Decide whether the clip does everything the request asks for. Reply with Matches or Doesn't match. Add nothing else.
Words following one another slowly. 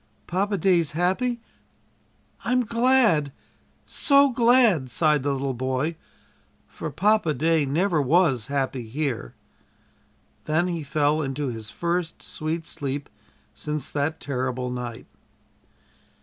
Matches